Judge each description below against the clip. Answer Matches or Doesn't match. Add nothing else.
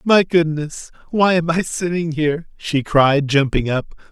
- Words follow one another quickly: Doesn't match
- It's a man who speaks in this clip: Matches